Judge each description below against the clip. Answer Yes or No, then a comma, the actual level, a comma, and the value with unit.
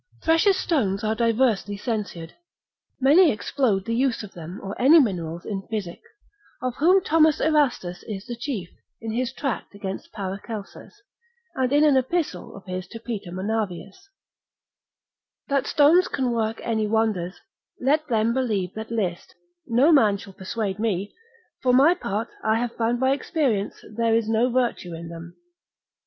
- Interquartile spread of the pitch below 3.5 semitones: No, average, 5.1 semitones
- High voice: Yes, high, 225 Hz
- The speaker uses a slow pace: No, average, 155 wpm